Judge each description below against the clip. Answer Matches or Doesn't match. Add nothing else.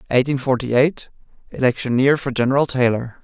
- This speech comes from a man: Matches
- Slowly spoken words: Matches